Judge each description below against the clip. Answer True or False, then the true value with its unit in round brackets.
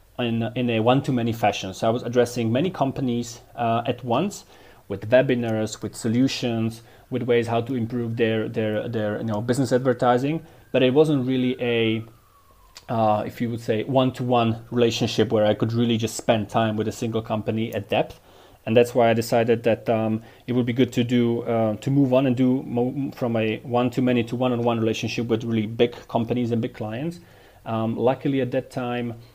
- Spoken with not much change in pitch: True (2.0 semitones)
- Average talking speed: False (190 wpm)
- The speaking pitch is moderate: False (120 Hz)